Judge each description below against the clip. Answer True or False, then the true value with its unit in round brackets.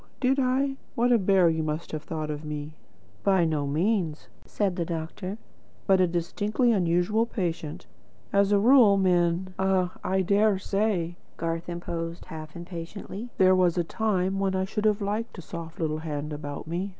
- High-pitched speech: False (180 Hz)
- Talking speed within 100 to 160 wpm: False (175 wpm)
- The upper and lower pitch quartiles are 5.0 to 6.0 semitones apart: False (3.5 semitones)